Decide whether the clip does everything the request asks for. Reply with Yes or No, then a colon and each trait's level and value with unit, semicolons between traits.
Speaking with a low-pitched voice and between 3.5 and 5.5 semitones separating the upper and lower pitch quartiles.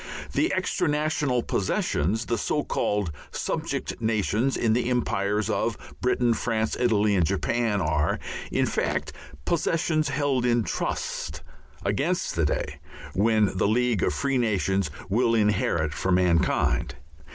Yes: low, 110 Hz; average, 4.2 semitones